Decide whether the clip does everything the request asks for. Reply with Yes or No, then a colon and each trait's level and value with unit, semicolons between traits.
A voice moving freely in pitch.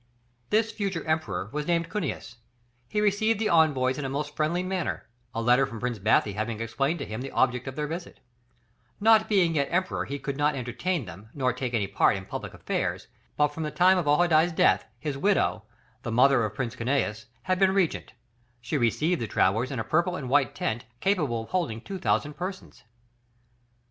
Yes: wide, 6.7 semitones